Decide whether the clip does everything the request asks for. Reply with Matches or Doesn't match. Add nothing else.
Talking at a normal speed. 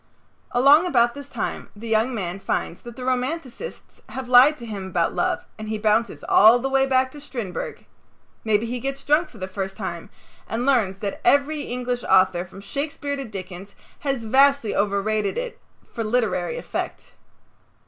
Matches